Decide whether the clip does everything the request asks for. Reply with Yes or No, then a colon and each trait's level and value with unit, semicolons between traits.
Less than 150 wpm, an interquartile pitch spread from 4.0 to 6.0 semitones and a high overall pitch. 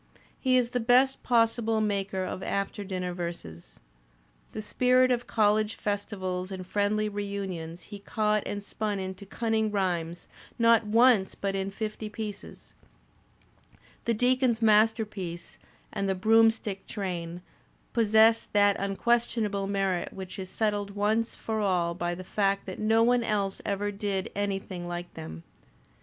No: average, 140 wpm; average, 2.7 semitones; high, 205 Hz